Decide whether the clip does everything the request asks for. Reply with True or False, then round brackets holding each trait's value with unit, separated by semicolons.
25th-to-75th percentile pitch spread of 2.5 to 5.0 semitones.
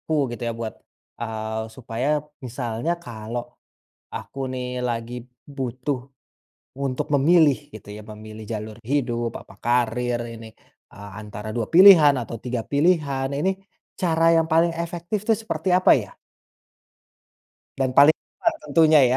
False (5.4 semitones)